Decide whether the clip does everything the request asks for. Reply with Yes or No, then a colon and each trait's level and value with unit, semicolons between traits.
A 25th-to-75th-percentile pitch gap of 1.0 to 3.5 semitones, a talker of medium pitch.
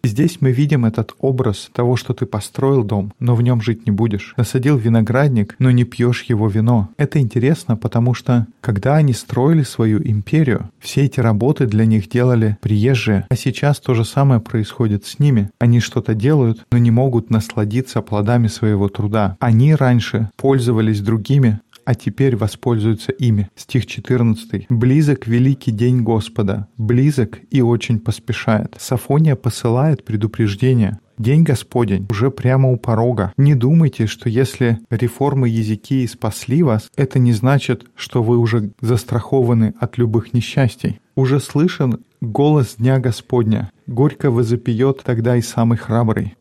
No: average, 2.9 semitones; low, 120 Hz